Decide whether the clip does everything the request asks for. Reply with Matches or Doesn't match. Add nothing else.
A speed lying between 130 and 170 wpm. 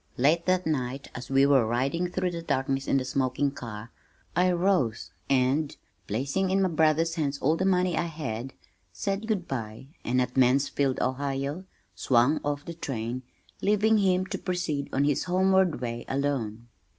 Matches